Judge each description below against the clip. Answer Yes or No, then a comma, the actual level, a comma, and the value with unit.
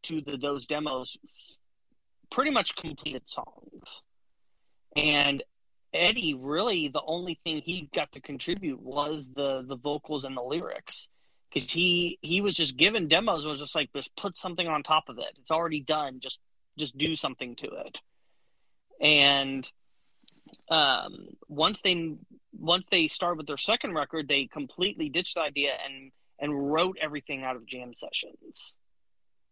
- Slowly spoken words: No, average, 155 wpm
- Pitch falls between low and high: Yes, medium, 150 Hz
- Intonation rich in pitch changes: No, average, 3.7 semitones